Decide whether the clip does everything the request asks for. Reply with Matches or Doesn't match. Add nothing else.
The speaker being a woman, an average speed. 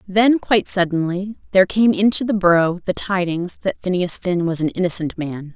Matches